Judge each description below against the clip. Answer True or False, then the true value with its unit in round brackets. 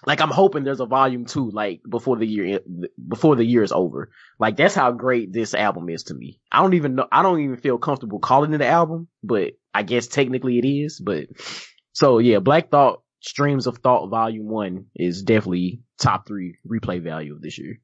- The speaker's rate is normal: False (210 wpm)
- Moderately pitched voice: False (125 Hz)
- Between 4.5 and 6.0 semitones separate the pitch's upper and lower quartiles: True (5.0 semitones)